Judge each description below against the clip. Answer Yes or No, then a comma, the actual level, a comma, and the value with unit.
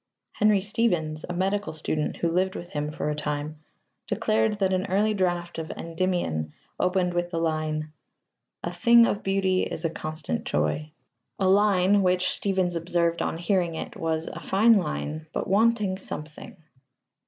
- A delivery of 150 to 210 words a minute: Yes, average, 155 wpm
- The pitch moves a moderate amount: Yes, average, 3.6 semitones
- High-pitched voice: No, medium, 175 Hz